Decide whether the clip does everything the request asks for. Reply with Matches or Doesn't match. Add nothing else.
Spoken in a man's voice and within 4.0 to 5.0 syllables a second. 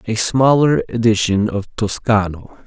Matches